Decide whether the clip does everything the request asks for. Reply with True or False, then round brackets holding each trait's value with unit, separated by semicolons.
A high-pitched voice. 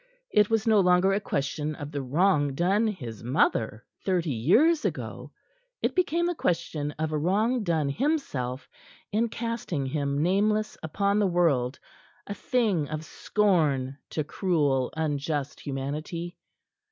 False (165 Hz)